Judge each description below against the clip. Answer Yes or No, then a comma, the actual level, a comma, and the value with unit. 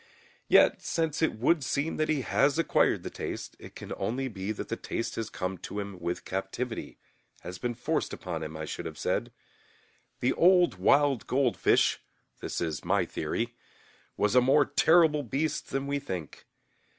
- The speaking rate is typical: Yes, average, 170 wpm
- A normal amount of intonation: No, wide, 7.2 semitones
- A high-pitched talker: No, low, 125 Hz